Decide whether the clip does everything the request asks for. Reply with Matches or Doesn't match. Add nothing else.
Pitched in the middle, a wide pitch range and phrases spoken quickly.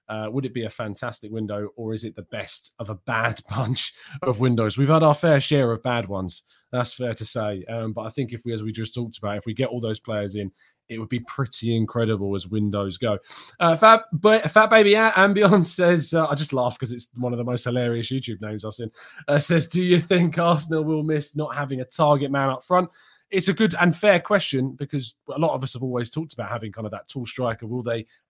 Doesn't match